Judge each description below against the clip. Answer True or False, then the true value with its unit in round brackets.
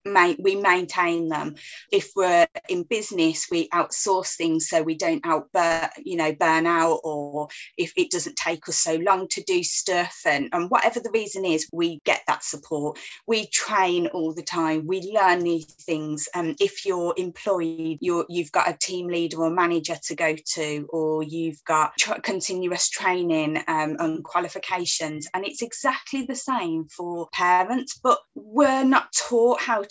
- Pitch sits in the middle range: True (175 Hz)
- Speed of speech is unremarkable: True (175 wpm)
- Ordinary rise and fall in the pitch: True (4.7 semitones)